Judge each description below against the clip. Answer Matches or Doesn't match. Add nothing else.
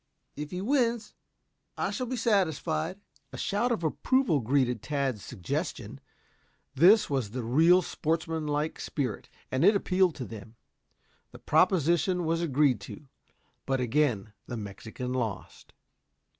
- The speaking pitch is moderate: Matches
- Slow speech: Matches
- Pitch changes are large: Matches